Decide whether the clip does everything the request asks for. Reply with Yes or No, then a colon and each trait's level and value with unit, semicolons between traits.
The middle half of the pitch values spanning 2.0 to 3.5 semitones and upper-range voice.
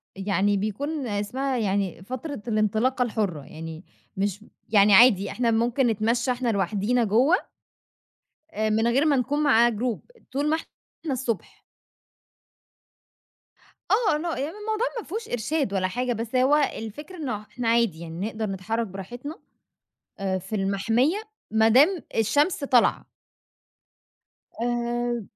No: average, 4.7 semitones; high, 235 Hz